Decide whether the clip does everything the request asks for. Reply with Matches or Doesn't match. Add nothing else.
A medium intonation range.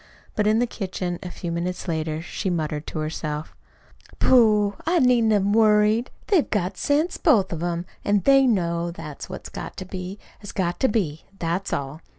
Matches